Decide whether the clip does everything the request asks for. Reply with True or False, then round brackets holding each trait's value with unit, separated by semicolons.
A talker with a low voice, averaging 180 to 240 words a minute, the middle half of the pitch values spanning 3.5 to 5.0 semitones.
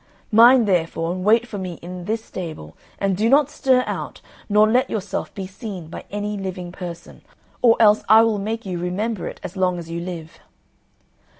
False (195 Hz; 190 wpm; 3.8 semitones)